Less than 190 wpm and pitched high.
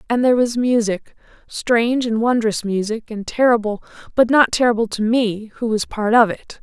Yes: average, 165 wpm; high, 225 Hz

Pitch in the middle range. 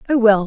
No: high, 225 Hz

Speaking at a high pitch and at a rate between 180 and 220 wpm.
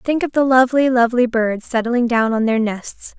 Yes: high, 240 Hz; fast, 205 wpm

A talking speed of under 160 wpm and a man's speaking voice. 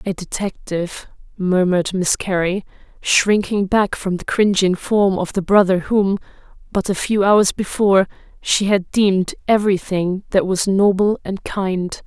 No: average, 150 wpm; female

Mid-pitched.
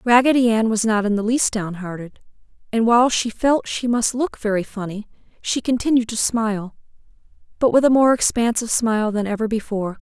No: high, 225 Hz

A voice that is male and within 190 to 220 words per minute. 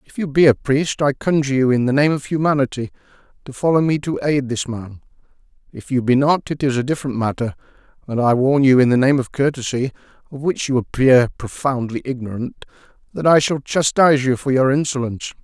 Yes: male; average, 200 wpm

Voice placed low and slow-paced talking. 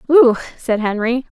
No: high, 245 Hz; slow, 130 wpm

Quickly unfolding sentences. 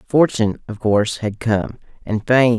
No: average, 160 wpm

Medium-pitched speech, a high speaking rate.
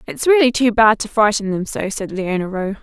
No: high, 215 Hz; fast, 235 wpm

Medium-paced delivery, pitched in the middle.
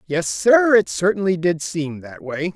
Yes: average, 190 wpm; medium, 170 Hz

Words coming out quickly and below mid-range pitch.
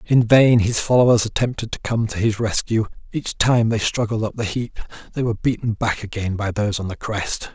Yes: fast, 215 wpm; low, 110 Hz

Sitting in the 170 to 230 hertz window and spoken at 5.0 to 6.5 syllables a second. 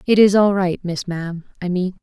Yes: medium, 185 Hz; 5.3 syllables/s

